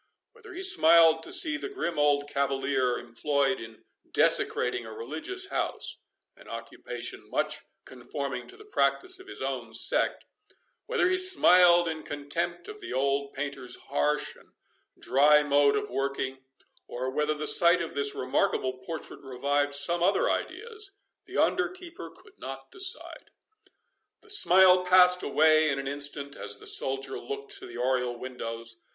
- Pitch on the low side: No, medium, 150 Hz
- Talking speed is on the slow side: No, average, 145 wpm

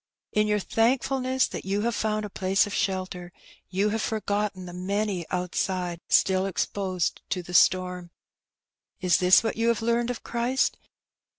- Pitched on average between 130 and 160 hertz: No, high, 200 Hz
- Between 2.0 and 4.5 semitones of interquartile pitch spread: Yes, average, 3.5 semitones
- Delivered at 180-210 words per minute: No, average, 165 wpm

